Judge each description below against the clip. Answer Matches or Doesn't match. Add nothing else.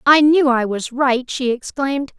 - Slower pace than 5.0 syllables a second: Matches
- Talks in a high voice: Matches